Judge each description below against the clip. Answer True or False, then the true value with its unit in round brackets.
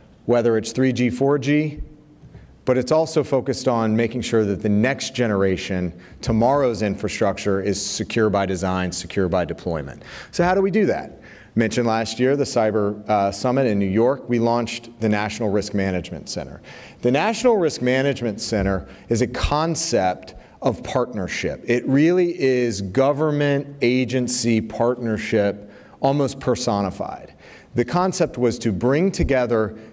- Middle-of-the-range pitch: False (120 Hz)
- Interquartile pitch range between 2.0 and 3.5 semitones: False (4.6 semitones)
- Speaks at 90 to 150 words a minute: True (140 wpm)